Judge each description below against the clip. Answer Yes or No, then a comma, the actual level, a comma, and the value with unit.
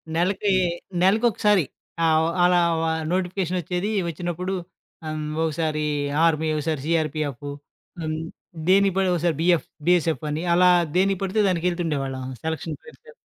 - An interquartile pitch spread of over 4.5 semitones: No, average, 2.9 semitones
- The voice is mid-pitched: Yes, medium, 170 Hz